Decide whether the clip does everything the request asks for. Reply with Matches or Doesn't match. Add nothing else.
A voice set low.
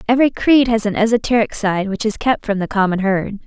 Doesn't match